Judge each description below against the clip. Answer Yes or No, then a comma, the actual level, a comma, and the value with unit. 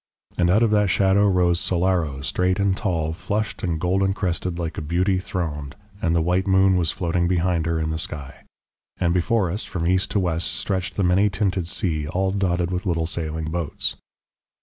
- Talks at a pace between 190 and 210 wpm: Yes, average, 195 wpm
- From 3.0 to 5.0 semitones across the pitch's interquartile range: No, narrow, 2.4 semitones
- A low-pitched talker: Yes, very low, 90 Hz